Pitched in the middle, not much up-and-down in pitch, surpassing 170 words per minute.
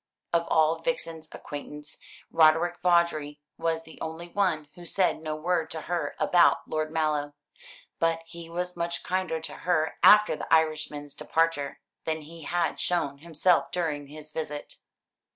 No: medium, 160 Hz; narrow, 1.9 semitones; average, 150 wpm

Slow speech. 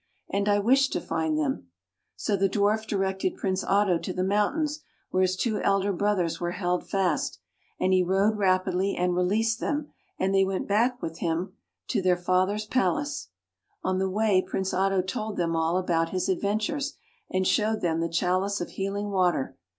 No: average, 180 wpm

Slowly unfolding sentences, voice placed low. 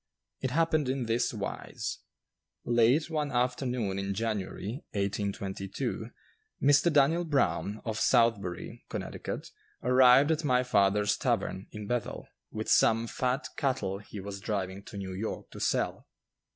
Yes: slow, 130 wpm; low, 115 Hz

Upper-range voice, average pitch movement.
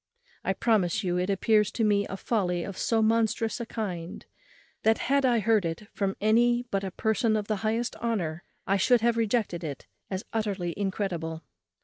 Yes: high, 210 Hz; average, 3.4 semitones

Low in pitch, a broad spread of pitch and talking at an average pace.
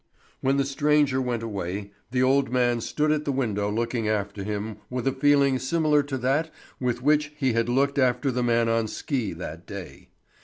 No: low, 125 Hz; average, 3.7 semitones; average, 190 wpm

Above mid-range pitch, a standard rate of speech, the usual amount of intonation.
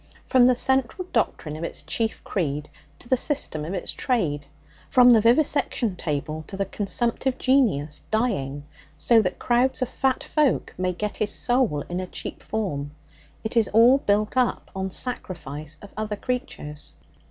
No: high, 215 Hz; average, 165 wpm; wide, 7.9 semitones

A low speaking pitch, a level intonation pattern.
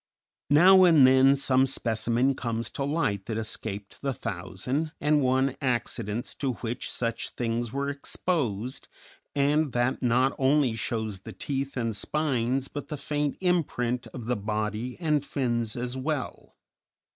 No: low, 130 Hz; average, 3.6 semitones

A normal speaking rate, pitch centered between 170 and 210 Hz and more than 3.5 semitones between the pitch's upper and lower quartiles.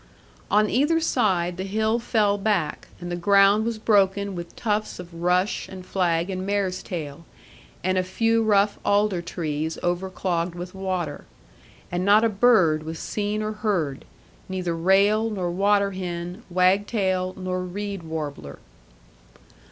No: average, 145 wpm; high, 190 Hz; average, 2.9 semitones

